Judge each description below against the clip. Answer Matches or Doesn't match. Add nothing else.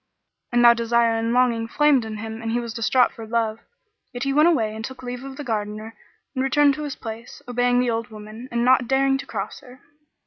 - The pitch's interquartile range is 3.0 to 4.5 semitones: Doesn't match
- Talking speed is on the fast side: Matches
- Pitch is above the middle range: Matches